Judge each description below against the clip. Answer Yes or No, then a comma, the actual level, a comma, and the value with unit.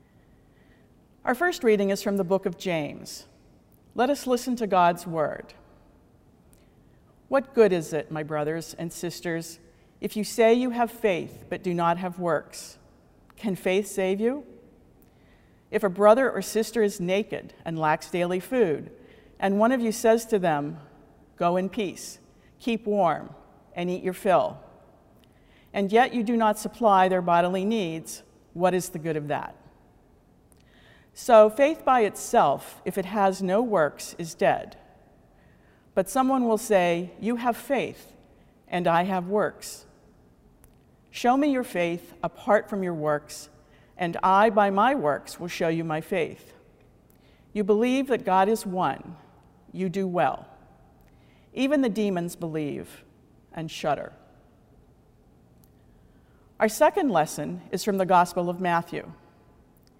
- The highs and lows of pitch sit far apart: No, average, 4.5 semitones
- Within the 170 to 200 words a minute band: No, average, 145 wpm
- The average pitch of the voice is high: Yes, high, 195 Hz